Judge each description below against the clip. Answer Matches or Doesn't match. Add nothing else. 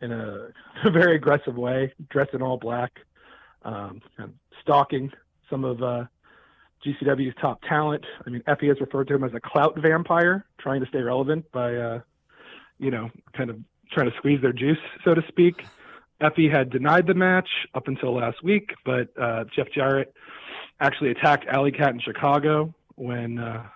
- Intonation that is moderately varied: Matches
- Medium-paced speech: Matches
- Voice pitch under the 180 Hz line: Matches